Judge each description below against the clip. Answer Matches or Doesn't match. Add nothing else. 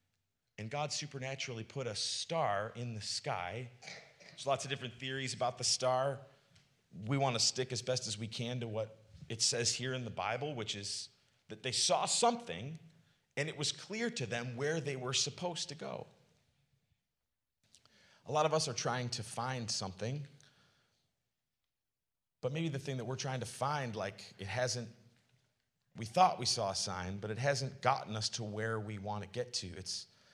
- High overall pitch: Doesn't match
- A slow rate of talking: Doesn't match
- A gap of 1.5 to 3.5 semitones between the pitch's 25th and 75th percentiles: Doesn't match